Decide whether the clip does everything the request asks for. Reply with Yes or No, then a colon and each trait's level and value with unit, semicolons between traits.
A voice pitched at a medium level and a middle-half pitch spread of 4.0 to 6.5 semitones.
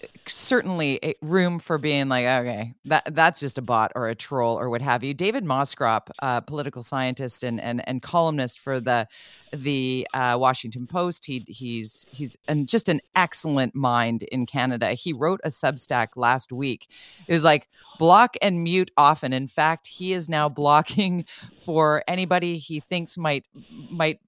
Yes: medium, 145 Hz; average, 4.8 semitones